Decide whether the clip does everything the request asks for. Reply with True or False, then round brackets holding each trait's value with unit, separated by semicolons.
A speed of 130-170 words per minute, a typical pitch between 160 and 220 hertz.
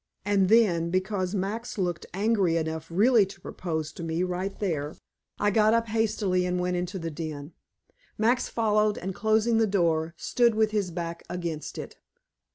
True (165 wpm; 185 Hz)